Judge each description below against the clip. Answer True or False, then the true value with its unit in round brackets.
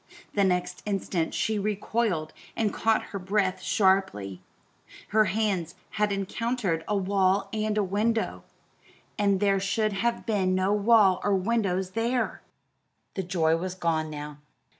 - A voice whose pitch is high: True (195 Hz)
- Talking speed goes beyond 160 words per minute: False (140 wpm)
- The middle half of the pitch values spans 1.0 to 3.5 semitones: True (2.5 semitones)